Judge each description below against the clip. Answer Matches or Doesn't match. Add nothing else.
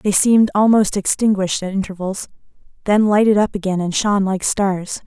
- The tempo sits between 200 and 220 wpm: Doesn't match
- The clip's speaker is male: Doesn't match